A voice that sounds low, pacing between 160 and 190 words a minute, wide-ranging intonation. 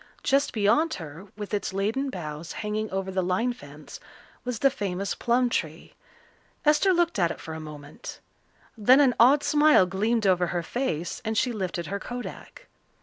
No: high, 210 Hz; average, 170 wpm; wide, 5.7 semitones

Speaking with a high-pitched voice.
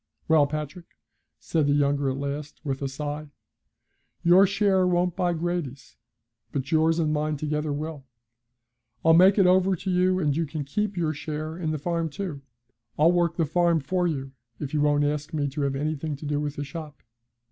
No: medium, 155 Hz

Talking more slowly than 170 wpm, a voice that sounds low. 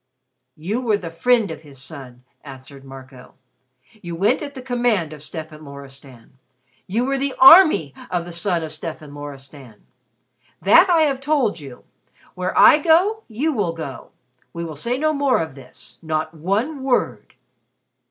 No: average, 160 wpm; medium, 170 Hz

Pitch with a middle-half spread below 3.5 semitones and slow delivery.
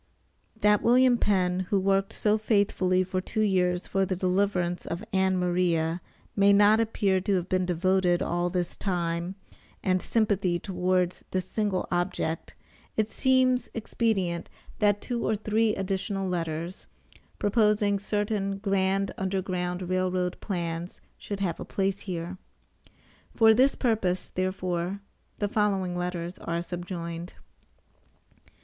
Yes: narrow, 2.4 semitones; slow, 130 wpm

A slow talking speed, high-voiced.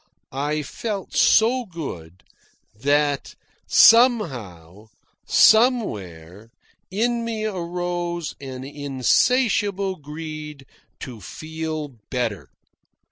No: slow, 75 wpm; medium, 155 Hz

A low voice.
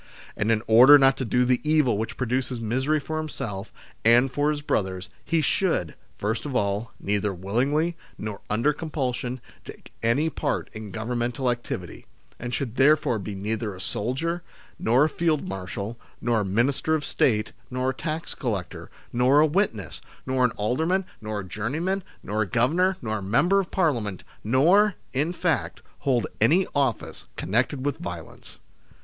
Yes: low, 125 Hz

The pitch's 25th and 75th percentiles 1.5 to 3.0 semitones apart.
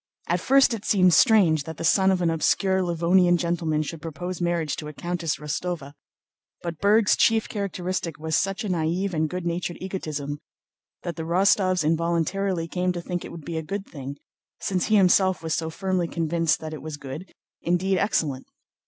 Yes: average, 2.7 semitones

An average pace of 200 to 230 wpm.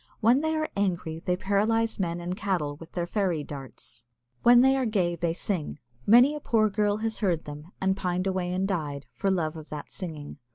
Yes: fast, 205 wpm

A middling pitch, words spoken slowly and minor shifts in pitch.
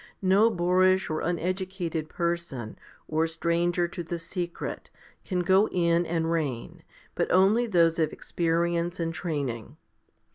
Yes: medium, 170 Hz; slow, 130 wpm; narrow, 1.8 semitones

